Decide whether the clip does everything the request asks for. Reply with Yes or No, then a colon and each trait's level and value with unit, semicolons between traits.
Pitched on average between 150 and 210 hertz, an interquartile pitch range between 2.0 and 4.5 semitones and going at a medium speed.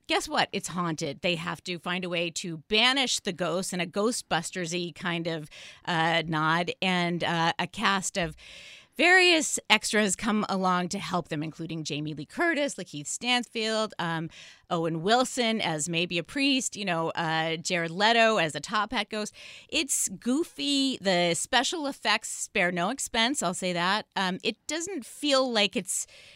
No: high, 190 Hz; wide, 5.4 semitones; average, 165 wpm